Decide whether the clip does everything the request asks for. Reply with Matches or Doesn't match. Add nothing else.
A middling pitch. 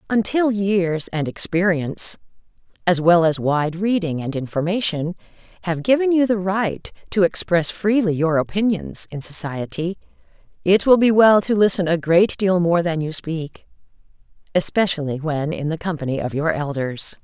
Matches